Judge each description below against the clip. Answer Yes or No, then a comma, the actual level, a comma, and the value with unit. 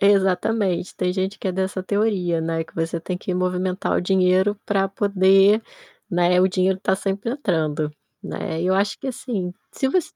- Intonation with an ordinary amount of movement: No, narrow, 1.9 semitones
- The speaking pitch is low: No, high, 190 Hz